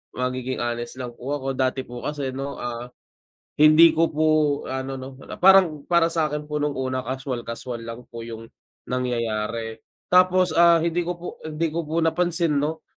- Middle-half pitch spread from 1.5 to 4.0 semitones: No, average, 4.8 semitones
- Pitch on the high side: No, medium, 140 Hz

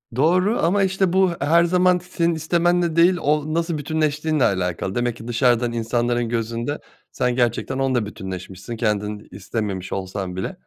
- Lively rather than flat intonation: Yes, wide, 7.2 semitones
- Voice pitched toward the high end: No, low, 130 Hz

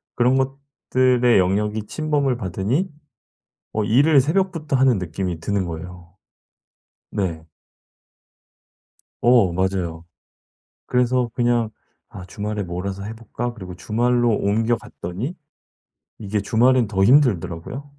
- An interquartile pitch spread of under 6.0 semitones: Yes, average, 5.2 semitones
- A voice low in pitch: Yes, low, 110 Hz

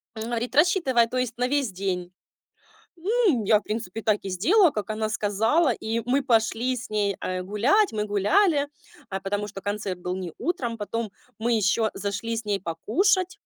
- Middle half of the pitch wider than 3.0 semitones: Yes, average, 4.3 semitones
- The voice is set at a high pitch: Yes, high, 225 Hz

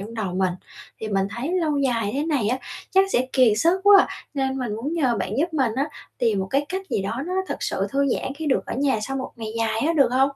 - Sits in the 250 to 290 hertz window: Yes, very high, 265 Hz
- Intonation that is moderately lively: Yes, average, 4.8 semitones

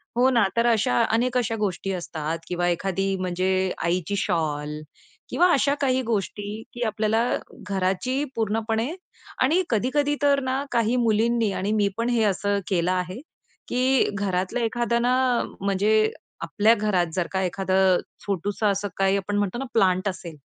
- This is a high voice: Yes, high, 205 Hz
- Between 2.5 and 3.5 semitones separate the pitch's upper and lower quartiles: No, average, 4.1 semitones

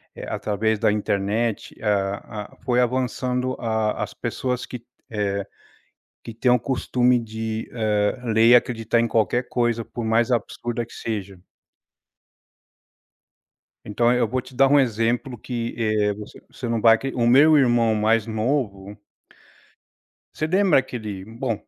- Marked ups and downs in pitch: No, narrow, 2.5 semitones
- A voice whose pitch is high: No, low, 115 Hz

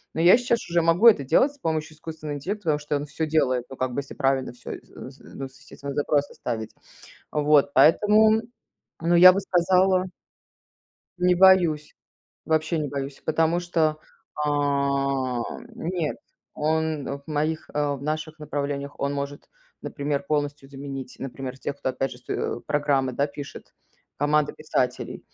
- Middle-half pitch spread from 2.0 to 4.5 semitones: Yes, average, 2.7 semitones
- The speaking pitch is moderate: Yes, medium, 150 Hz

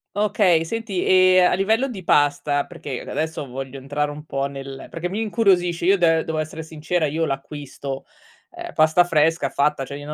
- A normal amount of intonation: Yes, average, 3.9 semitones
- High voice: No, medium, 160 Hz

